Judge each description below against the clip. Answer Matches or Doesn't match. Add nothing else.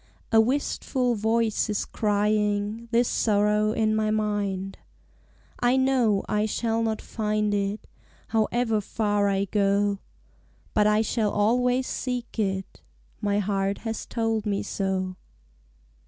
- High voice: Matches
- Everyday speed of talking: Doesn't match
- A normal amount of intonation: Doesn't match